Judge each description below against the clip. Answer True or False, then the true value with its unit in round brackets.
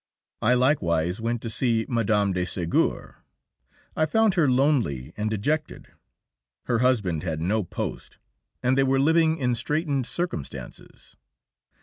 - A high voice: False (120 Hz)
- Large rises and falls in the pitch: True (6.3 semitones)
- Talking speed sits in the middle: False (130 wpm)